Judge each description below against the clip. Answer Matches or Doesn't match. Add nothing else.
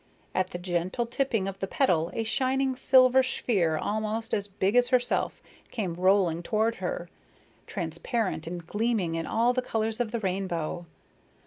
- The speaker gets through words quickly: Doesn't match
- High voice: Matches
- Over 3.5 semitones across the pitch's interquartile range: Matches